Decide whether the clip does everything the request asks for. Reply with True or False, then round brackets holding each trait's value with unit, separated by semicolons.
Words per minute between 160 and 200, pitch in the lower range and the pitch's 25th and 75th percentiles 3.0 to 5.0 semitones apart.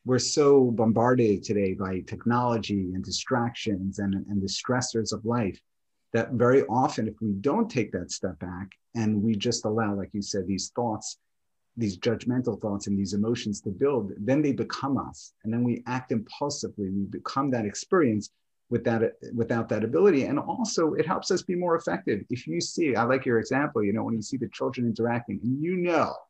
True (195 wpm; 115 Hz; 3.7 semitones)